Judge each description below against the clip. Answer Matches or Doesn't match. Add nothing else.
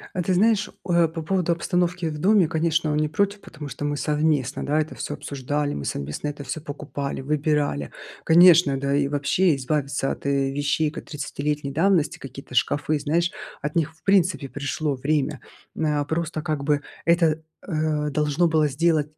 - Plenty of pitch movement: Doesn't match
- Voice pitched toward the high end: Doesn't match